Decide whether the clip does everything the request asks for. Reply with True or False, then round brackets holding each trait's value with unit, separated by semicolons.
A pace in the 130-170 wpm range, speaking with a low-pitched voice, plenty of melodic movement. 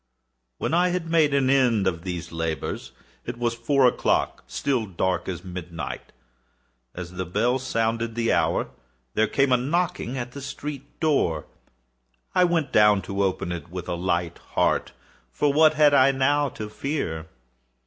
True (155 wpm; 120 Hz; 7.5 semitones)